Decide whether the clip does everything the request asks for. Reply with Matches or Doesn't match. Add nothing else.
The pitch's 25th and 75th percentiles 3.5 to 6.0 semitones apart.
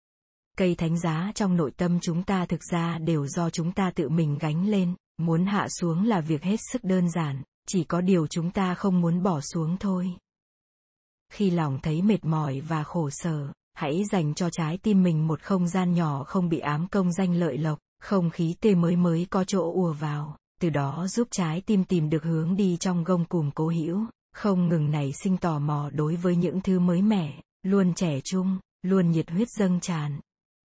Doesn't match